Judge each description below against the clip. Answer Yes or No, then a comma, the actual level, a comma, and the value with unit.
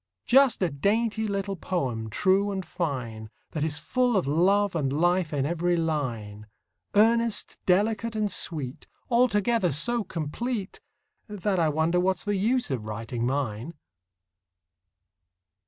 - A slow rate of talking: Yes, slow, 130 wpm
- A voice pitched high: No, medium, 175 Hz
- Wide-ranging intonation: Yes, wide, 6.5 semitones